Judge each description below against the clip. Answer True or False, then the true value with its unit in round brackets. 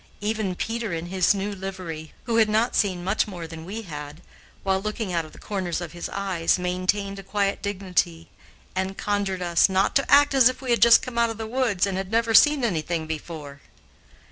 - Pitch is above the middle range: True (195 Hz)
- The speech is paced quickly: True (210 wpm)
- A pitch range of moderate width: True (4.1 semitones)